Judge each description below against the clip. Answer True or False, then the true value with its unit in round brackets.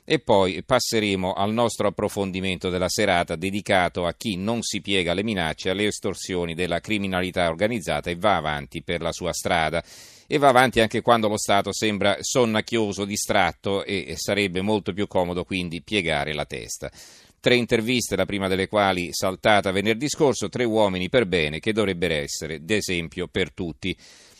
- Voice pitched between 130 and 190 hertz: False (100 Hz)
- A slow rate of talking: False (160 wpm)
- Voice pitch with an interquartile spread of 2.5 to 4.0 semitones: True (3.1 semitones)